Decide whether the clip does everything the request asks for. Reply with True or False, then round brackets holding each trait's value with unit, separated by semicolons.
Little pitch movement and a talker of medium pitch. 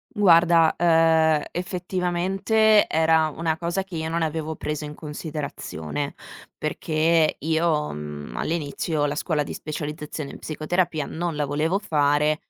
True (2.2 semitones; 160 Hz)